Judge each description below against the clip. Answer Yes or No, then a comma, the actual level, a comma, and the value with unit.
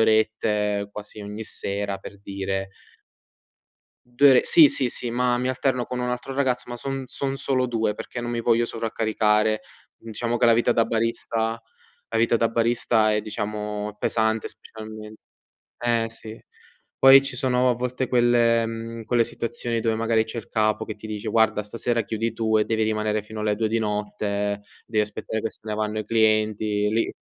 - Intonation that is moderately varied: No, narrow, 1.8 semitones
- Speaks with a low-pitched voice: Yes, low, 110 Hz